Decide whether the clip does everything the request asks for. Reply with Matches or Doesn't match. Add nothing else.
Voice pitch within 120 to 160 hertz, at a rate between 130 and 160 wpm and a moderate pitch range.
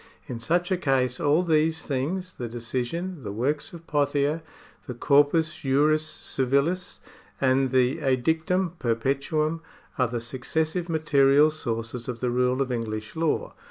Matches